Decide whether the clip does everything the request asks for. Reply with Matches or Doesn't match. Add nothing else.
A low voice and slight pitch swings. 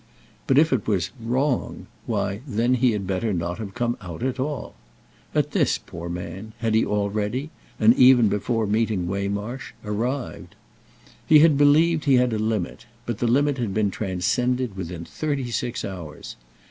Doesn't match